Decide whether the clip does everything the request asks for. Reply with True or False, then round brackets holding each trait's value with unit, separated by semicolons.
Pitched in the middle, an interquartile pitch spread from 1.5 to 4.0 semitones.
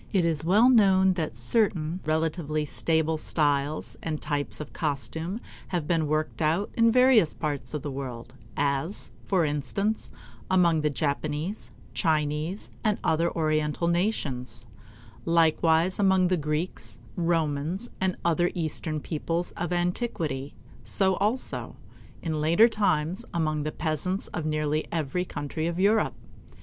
True (160 Hz; 3.4 semitones)